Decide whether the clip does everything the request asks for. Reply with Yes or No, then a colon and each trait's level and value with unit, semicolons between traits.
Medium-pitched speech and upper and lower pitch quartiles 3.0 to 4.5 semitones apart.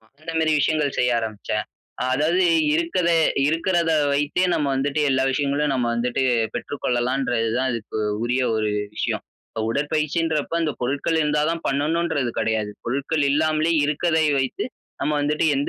Yes: medium, 145 Hz; average, 3.5 semitones